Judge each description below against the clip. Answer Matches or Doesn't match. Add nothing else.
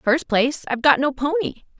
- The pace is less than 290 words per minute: Matches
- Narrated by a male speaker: Doesn't match